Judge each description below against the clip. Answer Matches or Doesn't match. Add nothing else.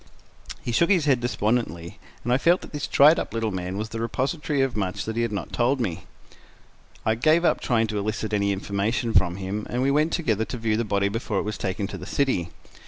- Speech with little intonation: Doesn't match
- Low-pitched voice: Matches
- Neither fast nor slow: Doesn't match